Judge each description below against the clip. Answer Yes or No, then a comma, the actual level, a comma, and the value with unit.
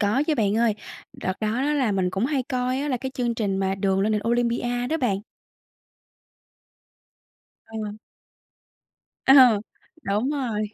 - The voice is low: No, high, 235 Hz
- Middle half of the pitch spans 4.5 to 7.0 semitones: No, average, 4.0 semitones